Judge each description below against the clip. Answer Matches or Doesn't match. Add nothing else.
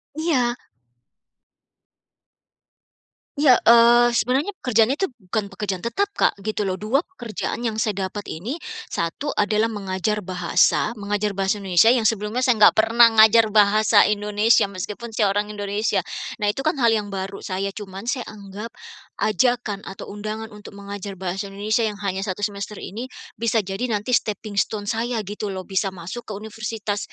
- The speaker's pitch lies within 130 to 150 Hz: Doesn't match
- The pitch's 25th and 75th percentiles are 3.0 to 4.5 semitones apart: Doesn't match